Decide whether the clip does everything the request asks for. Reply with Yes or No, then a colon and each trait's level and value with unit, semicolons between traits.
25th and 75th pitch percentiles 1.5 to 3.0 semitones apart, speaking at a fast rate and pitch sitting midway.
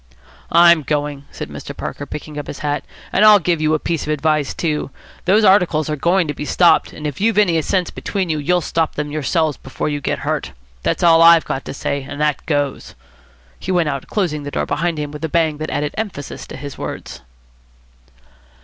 Yes: average, 2.7 semitones; fast, 215 wpm; medium, 155 Hz